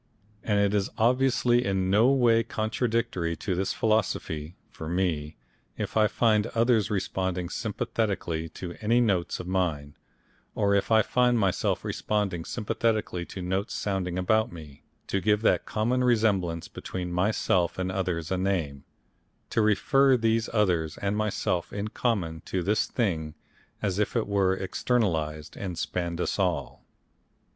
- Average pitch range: Yes, average, 4.0 semitones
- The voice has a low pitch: Yes, low, 100 Hz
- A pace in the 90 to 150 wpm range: Yes, average, 145 wpm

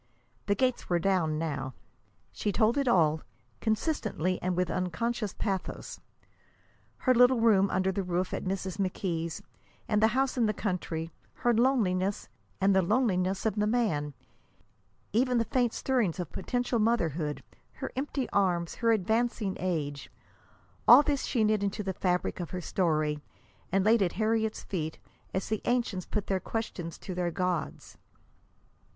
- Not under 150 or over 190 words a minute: Yes, average, 155 wpm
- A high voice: Yes, high, 195 Hz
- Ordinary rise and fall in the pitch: Yes, average, 4.3 semitones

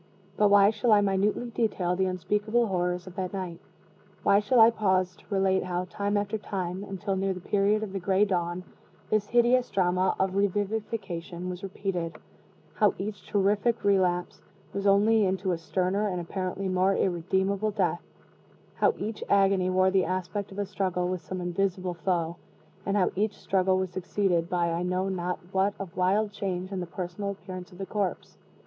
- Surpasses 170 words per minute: Yes, average, 180 wpm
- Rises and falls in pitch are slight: Yes, narrow, 1.9 semitones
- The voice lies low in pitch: No, high, 190 Hz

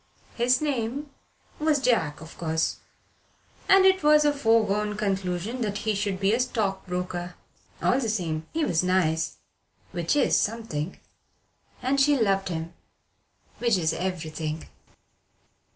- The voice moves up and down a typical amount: No, wide, 6.1 semitones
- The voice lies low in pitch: No, high, 205 Hz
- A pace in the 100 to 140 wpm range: Yes, slow, 135 wpm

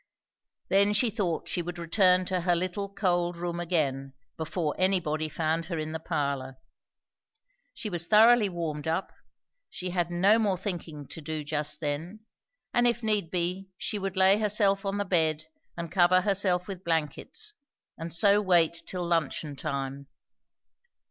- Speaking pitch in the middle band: Yes, medium, 175 Hz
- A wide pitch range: No, average, 3.6 semitones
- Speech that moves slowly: No, average, 155 wpm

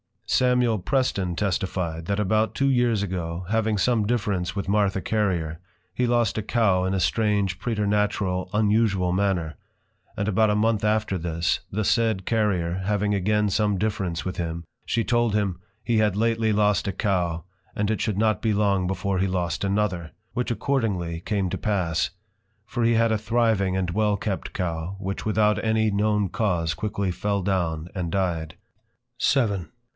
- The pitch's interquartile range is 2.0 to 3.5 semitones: Yes, average, 3.0 semitones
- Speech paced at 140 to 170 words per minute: Yes, average, 165 wpm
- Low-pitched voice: Yes, low, 100 Hz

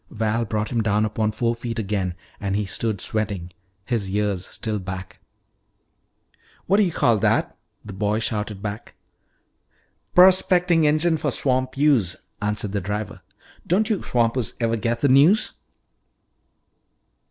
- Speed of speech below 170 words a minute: Yes, average, 140 wpm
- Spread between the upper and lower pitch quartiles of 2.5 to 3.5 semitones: No, average, 4.0 semitones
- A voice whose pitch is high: No, low, 110 Hz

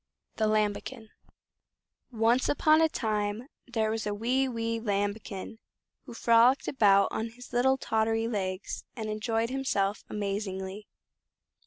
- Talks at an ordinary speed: No, slow, 125 wpm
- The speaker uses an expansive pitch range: No, average, 2.7 semitones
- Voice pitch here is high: Yes, high, 220 Hz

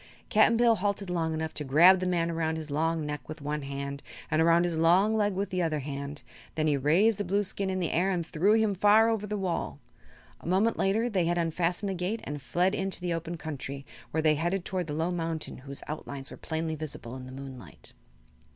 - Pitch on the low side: No, medium, 165 Hz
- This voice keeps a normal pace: No, fast, 225 wpm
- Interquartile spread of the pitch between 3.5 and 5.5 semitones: Yes, average, 4.1 semitones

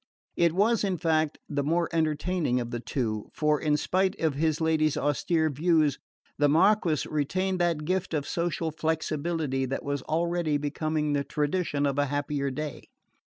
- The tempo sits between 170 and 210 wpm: No, average, 160 wpm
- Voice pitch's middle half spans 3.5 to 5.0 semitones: No, average, 2.8 semitones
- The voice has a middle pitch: Yes, medium, 155 Hz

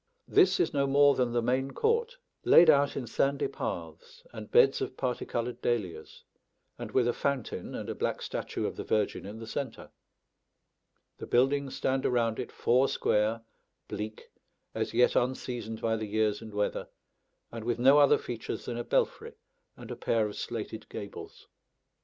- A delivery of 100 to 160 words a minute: No, average, 170 wpm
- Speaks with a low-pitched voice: Yes, low, 120 Hz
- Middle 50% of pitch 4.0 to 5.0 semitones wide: No, average, 3.6 semitones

